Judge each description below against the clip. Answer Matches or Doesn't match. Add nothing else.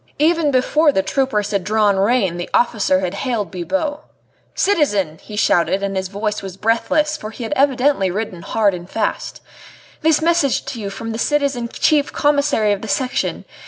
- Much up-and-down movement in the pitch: Matches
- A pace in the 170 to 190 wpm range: Matches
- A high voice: Matches